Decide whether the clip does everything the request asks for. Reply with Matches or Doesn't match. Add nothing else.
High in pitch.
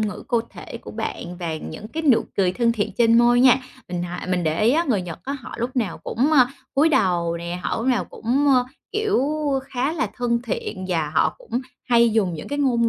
Matches